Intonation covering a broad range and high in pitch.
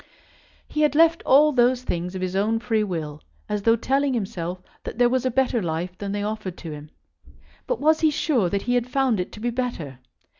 Yes: wide, 5.9 semitones; high, 225 Hz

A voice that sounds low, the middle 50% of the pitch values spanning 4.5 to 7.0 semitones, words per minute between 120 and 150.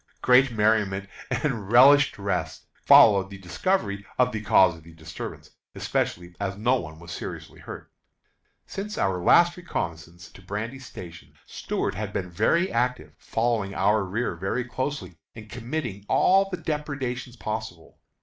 Yes: low, 105 Hz; average, 5.2 semitones; average, 140 wpm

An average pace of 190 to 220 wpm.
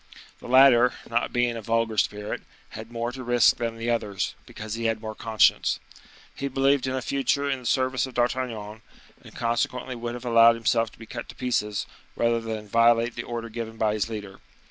Yes: average, 200 wpm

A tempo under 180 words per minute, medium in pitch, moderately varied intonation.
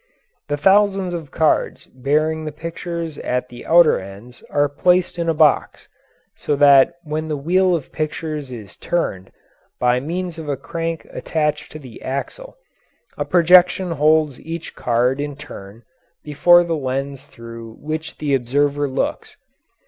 Yes: average, 150 wpm; medium, 150 Hz; average, 3.8 semitones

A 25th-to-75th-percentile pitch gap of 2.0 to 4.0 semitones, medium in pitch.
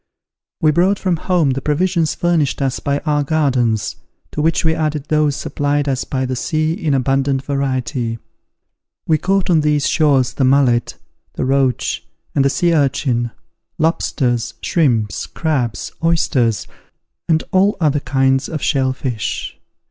Yes: average, 3.3 semitones; medium, 145 Hz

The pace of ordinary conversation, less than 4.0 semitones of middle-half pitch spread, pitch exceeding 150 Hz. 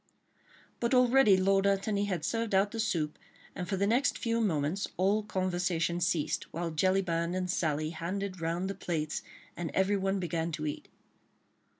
Yes: average, 160 wpm; average, 3.0 semitones; medium, 185 Hz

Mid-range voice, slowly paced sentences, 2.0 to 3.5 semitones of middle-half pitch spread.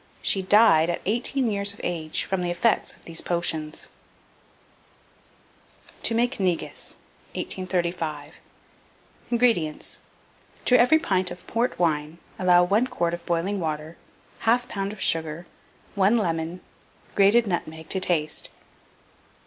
No: medium, 180 Hz; slow, 125 wpm; average, 4.3 semitones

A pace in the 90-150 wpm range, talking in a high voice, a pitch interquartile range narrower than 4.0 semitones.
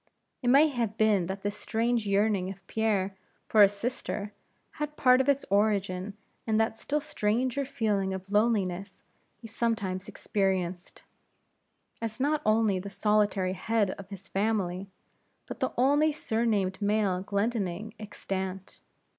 Yes: average, 140 wpm; high, 210 Hz; average, 2.9 semitones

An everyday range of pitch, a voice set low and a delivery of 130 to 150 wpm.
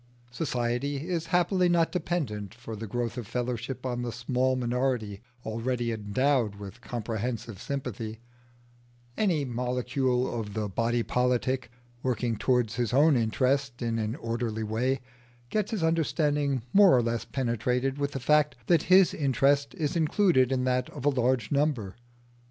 Yes: average, 3.4 semitones; low, 125 Hz; average, 145 wpm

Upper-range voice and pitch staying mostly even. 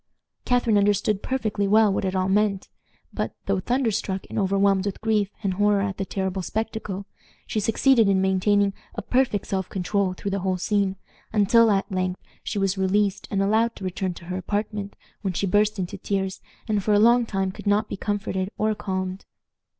Yes: high, 200 Hz; narrow, 1.8 semitones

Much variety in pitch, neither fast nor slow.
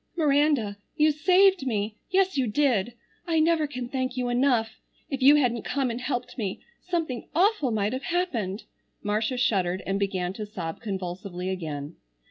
Yes: wide, 6.4 semitones; average, 160 wpm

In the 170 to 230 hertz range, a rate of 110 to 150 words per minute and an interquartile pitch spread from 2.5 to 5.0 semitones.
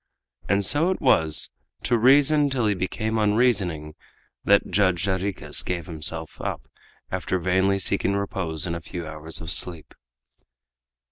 No: very low, 95 Hz; average, 140 wpm; average, 4.4 semitones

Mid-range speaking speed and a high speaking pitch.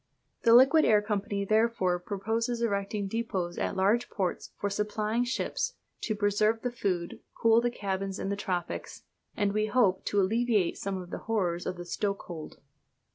Yes: average, 165 wpm; high, 205 Hz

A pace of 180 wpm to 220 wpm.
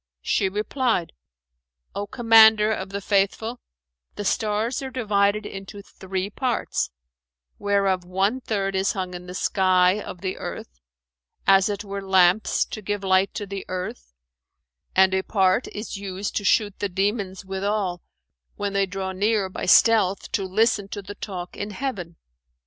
No: average, 155 wpm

